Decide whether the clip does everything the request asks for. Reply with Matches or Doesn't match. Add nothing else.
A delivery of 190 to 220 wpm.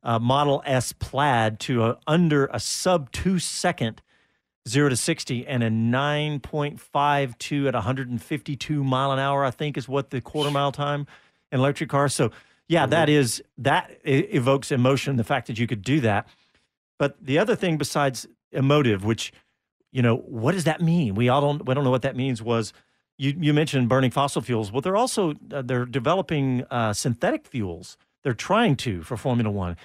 Matches